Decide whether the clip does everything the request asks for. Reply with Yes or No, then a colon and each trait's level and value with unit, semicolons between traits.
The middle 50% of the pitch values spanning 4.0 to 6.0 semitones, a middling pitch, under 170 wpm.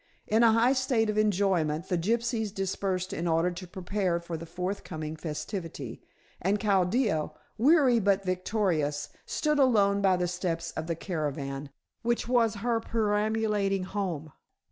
No: average, 4.5 semitones; high, 195 Hz; average, 145 wpm